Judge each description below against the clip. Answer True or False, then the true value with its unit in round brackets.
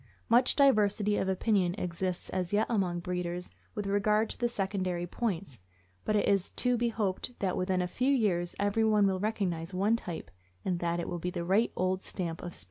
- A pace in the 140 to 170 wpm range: False (200 wpm)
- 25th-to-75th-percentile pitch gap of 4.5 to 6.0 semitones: False (3.2 semitones)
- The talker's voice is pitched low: False (190 Hz)